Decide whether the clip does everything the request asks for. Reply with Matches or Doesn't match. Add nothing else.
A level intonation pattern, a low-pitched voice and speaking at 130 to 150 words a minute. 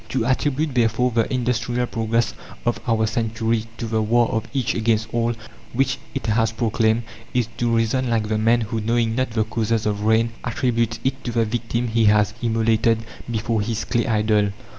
Doesn't match